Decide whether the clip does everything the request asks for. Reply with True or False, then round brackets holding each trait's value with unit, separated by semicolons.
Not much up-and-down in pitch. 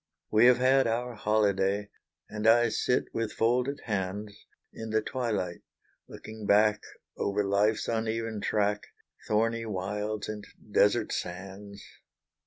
True (1.9 semitones)